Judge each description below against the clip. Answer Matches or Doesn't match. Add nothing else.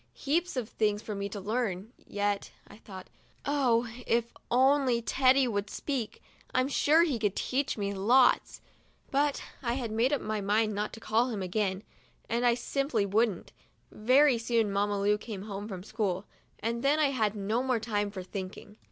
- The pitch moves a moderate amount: Matches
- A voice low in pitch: Doesn't match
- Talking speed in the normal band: Matches